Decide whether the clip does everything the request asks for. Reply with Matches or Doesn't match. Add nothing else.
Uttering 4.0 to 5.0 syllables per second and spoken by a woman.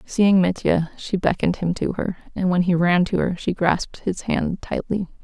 Matches